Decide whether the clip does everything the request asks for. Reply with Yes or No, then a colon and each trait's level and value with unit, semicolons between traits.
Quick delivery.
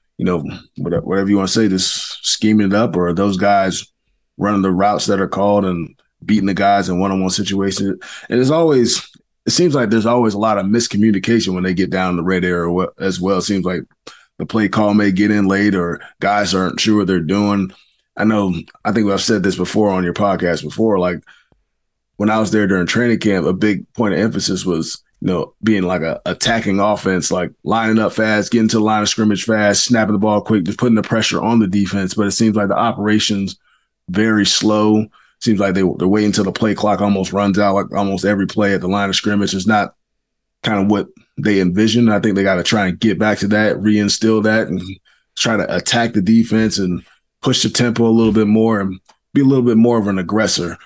Yes: fast, 225 wpm